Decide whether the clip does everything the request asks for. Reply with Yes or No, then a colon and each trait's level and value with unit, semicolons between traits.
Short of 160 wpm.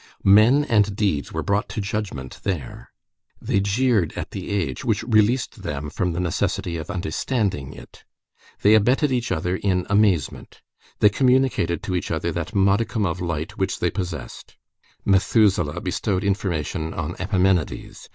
Yes: average, 150 wpm